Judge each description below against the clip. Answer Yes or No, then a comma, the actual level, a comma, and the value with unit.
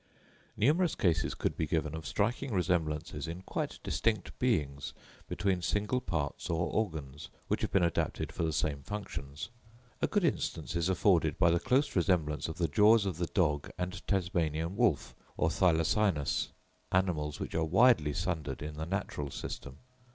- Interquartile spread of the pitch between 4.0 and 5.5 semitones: Yes, average, 4.5 semitones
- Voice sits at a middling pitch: No, very low, 85 Hz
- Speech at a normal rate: Yes, average, 160 wpm